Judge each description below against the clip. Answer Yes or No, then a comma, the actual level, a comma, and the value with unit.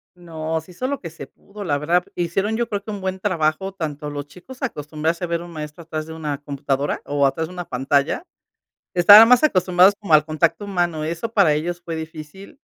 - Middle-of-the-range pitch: Yes, medium, 170 Hz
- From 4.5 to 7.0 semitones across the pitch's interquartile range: No, average, 3.9 semitones